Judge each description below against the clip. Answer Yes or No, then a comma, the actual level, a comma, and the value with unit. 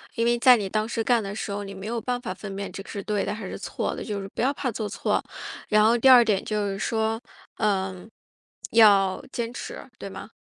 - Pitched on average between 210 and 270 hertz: Yes, high, 215 Hz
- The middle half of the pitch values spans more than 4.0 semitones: No, average, 2.7 semitones